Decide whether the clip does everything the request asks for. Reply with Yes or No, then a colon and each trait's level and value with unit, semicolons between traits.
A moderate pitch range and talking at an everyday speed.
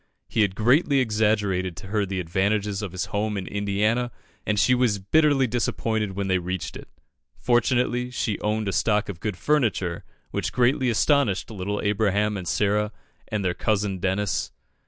Yes: average, 3.0 semitones; average, 165 wpm